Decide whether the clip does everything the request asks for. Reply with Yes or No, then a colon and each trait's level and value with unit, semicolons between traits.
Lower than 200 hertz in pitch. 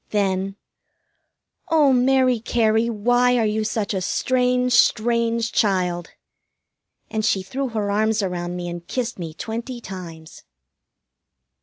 No: high, 220 Hz